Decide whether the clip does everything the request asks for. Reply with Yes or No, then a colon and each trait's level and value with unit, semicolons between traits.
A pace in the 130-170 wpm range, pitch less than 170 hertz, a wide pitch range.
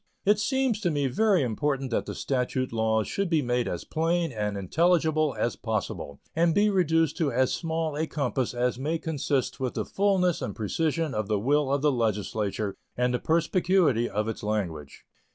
No: average, 185 wpm; medium, 140 Hz; wide, 6.5 semitones